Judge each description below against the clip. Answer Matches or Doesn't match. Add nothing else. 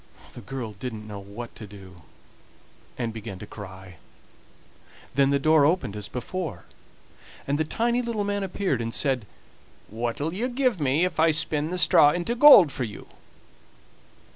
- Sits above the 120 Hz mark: Matches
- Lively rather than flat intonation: Matches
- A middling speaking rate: Matches